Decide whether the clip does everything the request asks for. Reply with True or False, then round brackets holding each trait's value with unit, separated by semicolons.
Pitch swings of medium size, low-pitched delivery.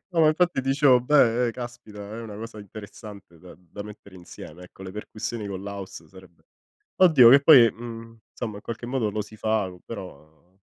True (3.9 semitones; 110 Hz)